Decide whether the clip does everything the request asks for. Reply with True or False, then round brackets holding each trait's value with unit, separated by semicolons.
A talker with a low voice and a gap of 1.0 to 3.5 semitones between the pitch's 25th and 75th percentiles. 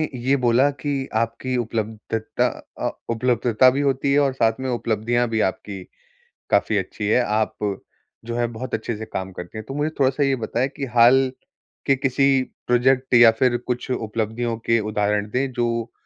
True (120 Hz; 2.9 semitones)